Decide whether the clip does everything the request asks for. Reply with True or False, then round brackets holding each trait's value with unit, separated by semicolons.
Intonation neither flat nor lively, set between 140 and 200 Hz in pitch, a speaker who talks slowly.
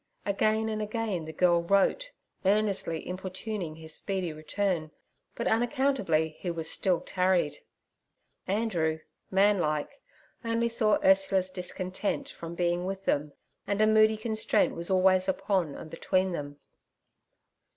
True (3.7 semitones; 185 Hz; 125 wpm)